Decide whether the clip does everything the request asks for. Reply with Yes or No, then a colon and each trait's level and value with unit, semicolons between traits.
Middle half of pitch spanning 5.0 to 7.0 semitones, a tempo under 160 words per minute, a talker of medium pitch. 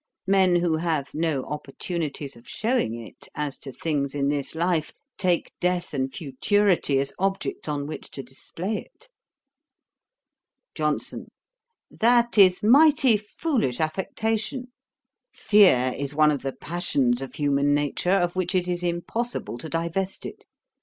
Yes: wide, 5.5 semitones; average, 140 wpm; medium, 165 Hz